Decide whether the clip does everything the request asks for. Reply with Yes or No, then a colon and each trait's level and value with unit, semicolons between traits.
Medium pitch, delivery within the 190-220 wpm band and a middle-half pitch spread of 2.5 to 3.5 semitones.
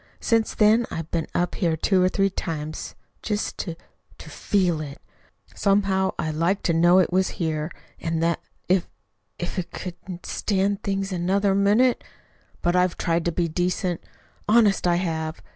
No: medium, 180 Hz; average, 170 wpm; average, 2.8 semitones